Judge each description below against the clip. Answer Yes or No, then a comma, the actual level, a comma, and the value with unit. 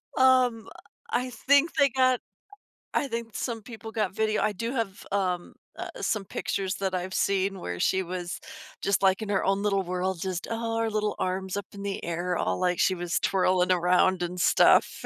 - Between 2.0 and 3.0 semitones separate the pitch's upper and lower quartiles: No, average, 3.7 semitones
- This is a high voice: Yes, high, 195 Hz